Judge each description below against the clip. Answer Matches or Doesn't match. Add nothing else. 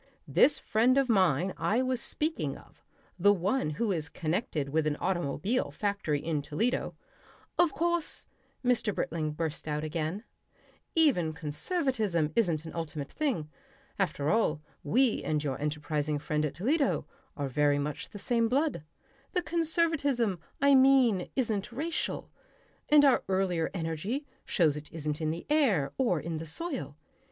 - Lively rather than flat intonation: Matches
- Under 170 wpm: Matches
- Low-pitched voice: Doesn't match